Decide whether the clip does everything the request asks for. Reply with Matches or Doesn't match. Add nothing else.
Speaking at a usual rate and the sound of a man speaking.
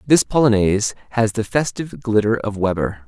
Matches